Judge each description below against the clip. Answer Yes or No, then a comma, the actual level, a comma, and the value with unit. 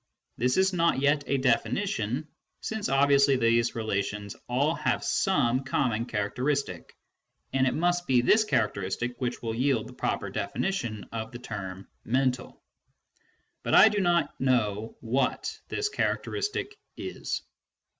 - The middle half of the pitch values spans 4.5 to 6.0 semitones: Yes, average, 5.0 semitones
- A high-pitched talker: No, low, 130 Hz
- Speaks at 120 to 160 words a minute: Yes, slow, 135 wpm